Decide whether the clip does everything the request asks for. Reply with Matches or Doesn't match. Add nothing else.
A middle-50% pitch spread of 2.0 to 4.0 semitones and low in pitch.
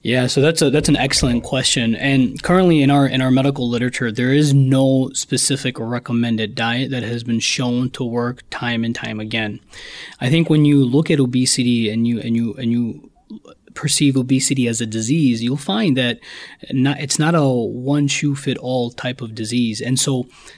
Matches